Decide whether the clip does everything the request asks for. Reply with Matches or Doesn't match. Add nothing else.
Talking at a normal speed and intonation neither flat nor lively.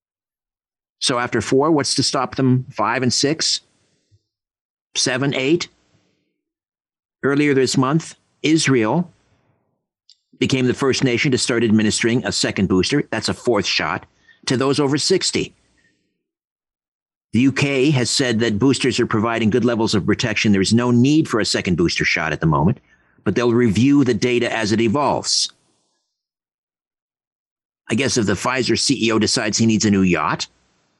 Matches